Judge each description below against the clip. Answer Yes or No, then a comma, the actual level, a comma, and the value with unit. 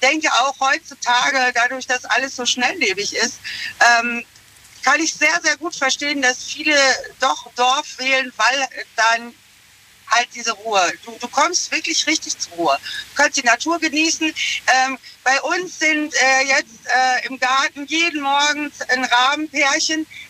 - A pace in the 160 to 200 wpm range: No, average, 150 wpm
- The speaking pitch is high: Yes, very high, 275 Hz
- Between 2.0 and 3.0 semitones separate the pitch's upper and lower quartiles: No, average, 3.7 semitones